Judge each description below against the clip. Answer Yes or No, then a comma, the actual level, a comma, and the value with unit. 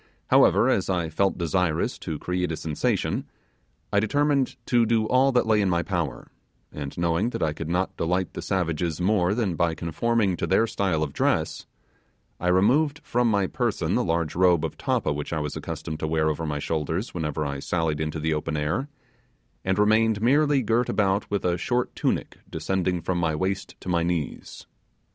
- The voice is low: Yes, very low, 90 Hz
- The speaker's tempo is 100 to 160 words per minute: No, average, 190 wpm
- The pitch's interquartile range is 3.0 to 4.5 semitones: No, average, 4.9 semitones